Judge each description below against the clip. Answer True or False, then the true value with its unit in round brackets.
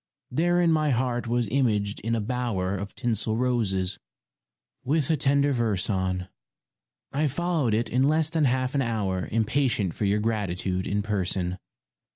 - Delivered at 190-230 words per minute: False (155 wpm)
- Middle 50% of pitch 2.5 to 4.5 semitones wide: False (5.3 semitones)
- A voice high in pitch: False (115 Hz)